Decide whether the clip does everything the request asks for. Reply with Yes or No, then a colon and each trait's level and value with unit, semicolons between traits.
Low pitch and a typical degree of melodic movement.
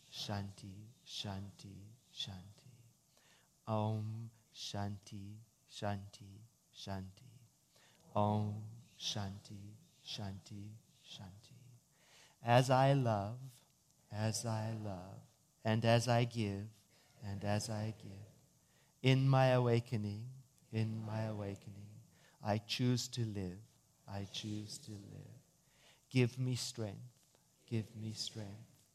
Yes: low, 110 Hz; average, 3.9 semitones